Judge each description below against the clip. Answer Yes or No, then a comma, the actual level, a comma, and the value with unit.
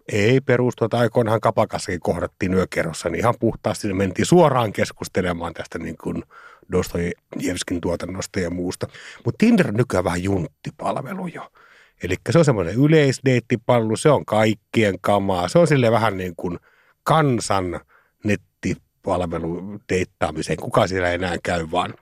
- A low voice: Yes, low, 105 Hz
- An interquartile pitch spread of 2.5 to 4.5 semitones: No, average, 5.2 semitones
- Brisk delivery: No, average, 140 wpm